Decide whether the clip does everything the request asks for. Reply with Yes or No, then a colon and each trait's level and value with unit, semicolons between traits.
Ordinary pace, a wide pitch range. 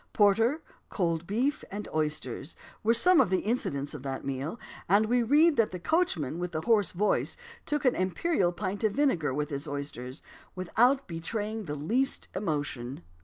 Yes: average, 170 wpm; wide, 7.6 semitones